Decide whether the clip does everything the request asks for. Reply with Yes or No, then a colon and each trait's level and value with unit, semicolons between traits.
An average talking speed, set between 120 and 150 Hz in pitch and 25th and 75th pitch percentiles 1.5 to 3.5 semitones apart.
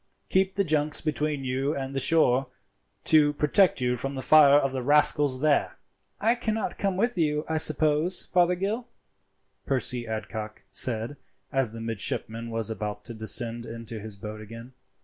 No: average, 160 wpm; low, 135 Hz; average, 5.2 semitones